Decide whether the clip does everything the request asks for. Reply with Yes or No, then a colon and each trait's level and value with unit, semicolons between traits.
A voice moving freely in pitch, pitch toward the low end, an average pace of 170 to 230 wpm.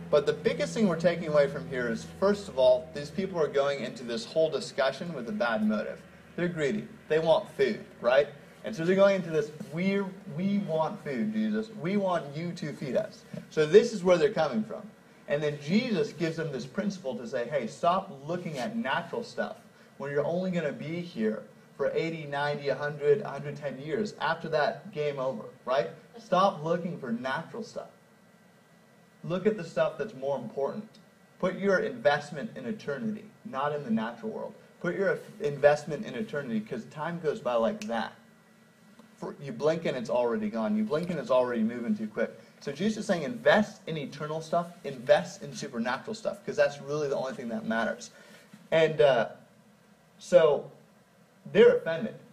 No: wide, 5.8 semitones; high, 195 Hz; average, 185 wpm